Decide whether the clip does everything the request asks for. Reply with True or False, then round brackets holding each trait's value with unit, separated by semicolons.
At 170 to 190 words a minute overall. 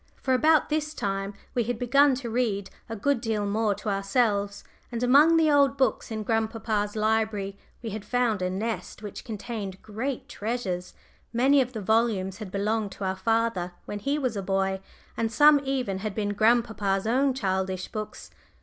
True (175 wpm)